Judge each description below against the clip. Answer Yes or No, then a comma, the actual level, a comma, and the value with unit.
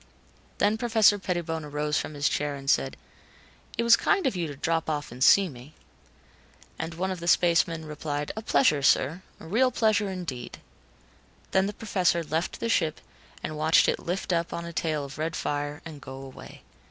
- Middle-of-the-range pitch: Yes, medium, 165 Hz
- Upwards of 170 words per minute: Yes, average, 190 wpm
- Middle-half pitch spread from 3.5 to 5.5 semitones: Yes, average, 4.3 semitones